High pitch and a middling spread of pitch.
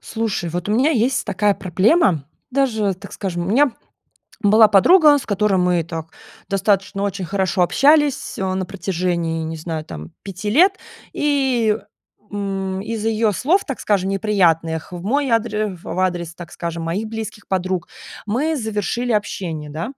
Yes: high, 200 Hz; average, 4.2 semitones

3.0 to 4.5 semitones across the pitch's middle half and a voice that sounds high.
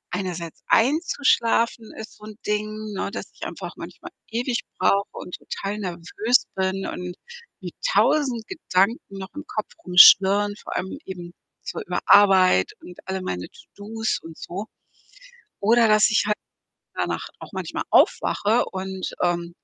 Yes: average, 3.3 semitones; high, 200 Hz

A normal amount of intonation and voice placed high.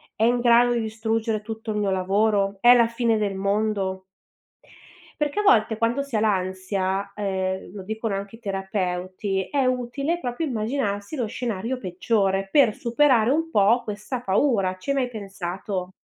Yes: average, 3.6 semitones; high, 215 Hz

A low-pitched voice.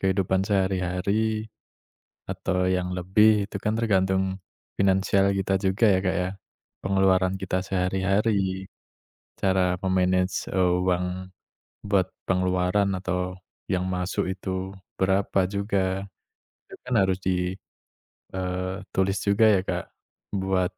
Yes: very low, 95 Hz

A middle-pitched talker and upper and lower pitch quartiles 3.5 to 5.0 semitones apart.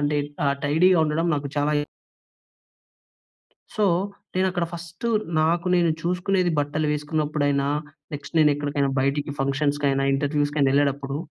No: medium, 150 Hz; average, 2.8 semitones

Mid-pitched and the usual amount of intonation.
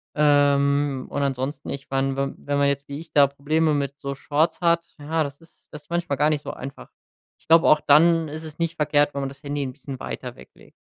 No: medium, 145 Hz; narrow, 1.9 semitones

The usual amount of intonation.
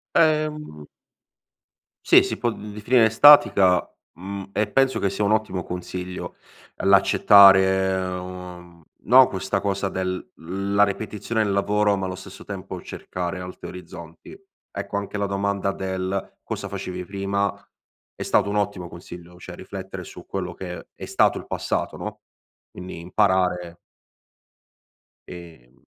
No: narrow, 2.0 semitones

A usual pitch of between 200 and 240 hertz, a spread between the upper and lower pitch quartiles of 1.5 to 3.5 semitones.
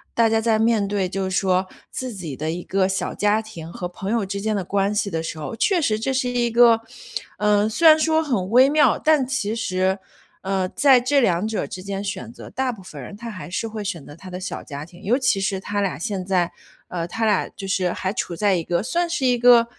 No: high, 205 Hz; average, 4.1 semitones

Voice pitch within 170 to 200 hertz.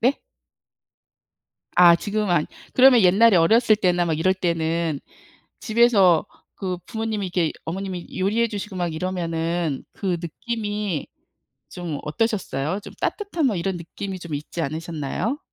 Yes: medium, 185 Hz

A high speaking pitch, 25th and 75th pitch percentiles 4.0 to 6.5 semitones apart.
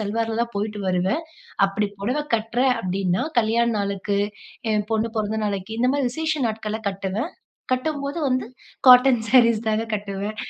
No: high, 220 Hz; average, 3.6 semitones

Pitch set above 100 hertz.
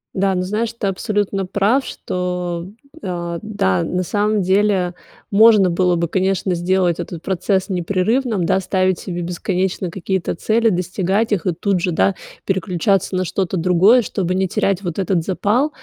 Yes: medium, 185 Hz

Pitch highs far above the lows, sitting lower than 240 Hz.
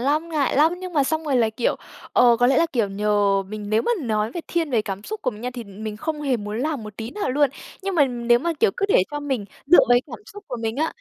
No: wide, 6.1 semitones; very high, 250 Hz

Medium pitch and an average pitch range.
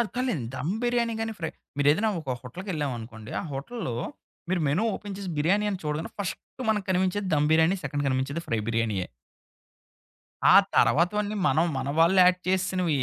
No: medium, 170 Hz; wide, 6.1 semitones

